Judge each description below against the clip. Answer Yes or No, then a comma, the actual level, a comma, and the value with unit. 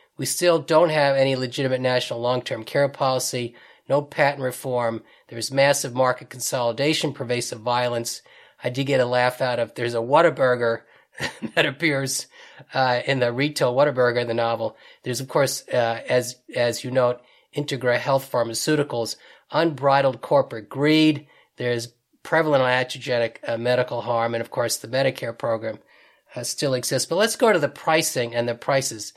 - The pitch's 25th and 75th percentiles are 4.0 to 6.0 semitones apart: No, average, 2.7 semitones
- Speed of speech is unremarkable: Yes, average, 160 wpm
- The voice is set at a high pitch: No, low, 125 Hz